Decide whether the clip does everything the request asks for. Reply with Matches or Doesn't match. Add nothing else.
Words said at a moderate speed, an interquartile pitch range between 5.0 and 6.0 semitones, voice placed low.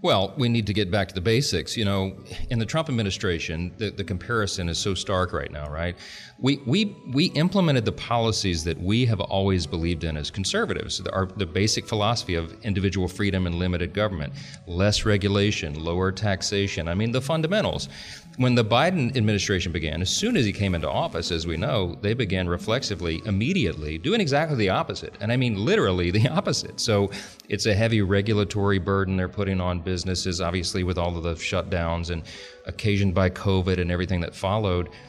Doesn't match